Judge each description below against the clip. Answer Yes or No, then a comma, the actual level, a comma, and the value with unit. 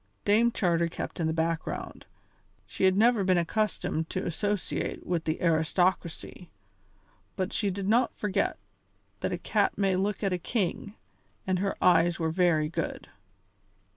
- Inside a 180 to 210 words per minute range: No, average, 150 wpm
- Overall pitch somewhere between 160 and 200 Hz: Yes, medium, 185 Hz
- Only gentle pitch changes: No, average, 3.3 semitones